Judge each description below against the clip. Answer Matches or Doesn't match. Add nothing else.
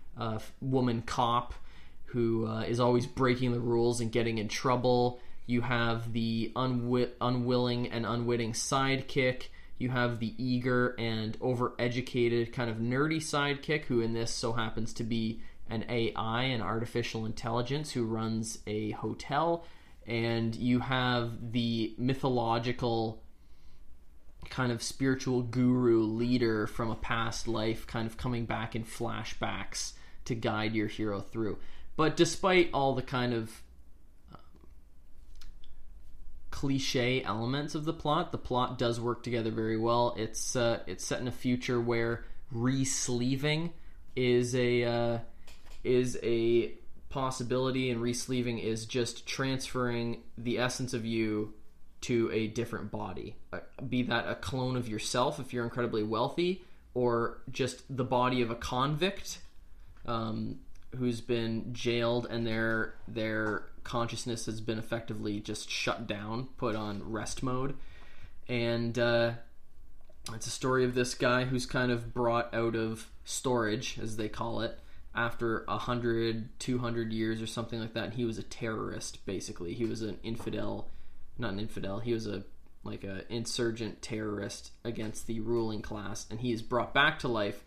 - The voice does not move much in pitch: Matches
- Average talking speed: Matches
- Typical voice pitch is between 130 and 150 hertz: Doesn't match